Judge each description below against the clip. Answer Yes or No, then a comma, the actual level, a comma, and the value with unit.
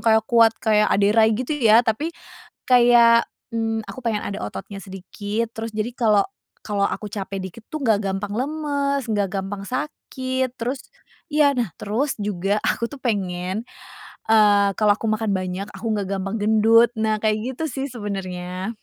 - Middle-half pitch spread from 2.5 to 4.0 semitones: Yes, average, 2.8 semitones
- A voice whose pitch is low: No, high, 215 Hz